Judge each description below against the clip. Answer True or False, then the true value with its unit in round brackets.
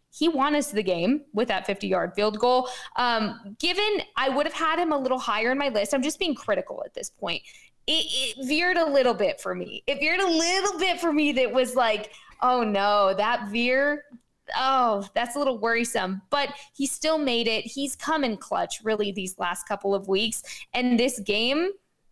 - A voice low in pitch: False (255 Hz)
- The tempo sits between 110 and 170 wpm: False (205 wpm)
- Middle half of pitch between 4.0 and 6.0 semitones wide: True (5.3 semitones)